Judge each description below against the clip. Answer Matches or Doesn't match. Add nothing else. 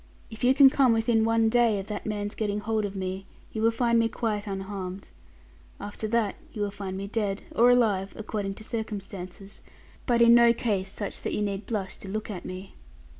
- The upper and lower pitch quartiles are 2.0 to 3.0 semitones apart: Matches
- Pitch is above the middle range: Matches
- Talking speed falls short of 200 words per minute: Doesn't match